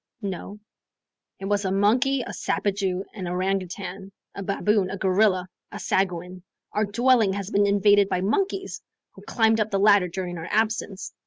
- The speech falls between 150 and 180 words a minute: Yes, average, 160 wpm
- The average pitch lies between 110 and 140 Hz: No, high, 200 Hz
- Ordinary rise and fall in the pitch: No, narrow, 2.1 semitones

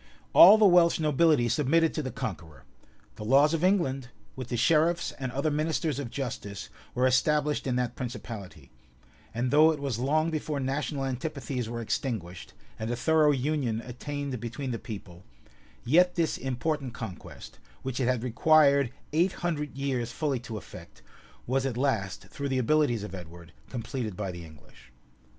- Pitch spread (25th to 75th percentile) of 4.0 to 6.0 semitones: Yes, average, 4.5 semitones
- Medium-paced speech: Yes, average, 165 wpm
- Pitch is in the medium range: No, low, 130 Hz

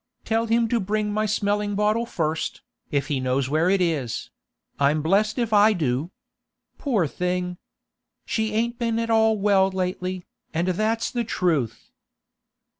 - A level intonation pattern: No, average, 4.9 semitones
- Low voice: No, high, 195 Hz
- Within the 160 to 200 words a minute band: No, average, 145 wpm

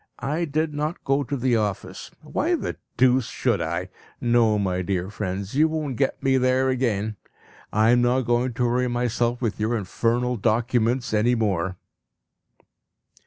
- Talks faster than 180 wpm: No, average, 160 wpm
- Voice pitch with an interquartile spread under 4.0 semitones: Yes, average, 3.3 semitones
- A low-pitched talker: Yes, low, 120 Hz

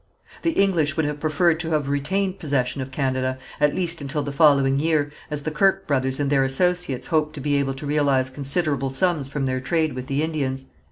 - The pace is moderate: No, fast, 210 wpm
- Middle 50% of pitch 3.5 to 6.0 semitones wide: No, average, 2.9 semitones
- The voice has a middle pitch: Yes, medium, 145 Hz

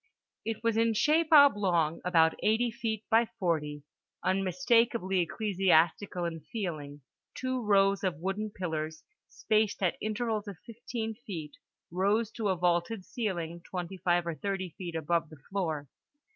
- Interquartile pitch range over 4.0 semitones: Yes, average, 4.5 semitones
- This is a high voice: Yes, high, 195 Hz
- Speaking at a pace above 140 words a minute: No, slow, 135 wpm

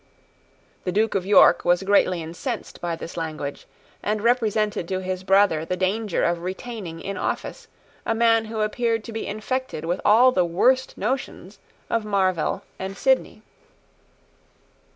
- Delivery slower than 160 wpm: Yes, average, 150 wpm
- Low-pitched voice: No, high, 200 Hz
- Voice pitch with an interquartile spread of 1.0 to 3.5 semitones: No, average, 3.9 semitones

